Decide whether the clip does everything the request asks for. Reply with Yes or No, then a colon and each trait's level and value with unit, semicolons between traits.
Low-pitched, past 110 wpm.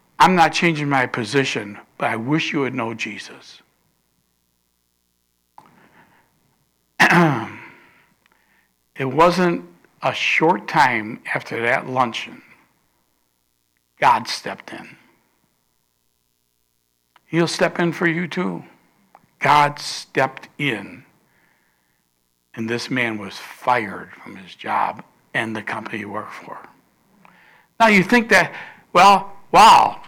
No: low, 120 Hz; slow, 105 wpm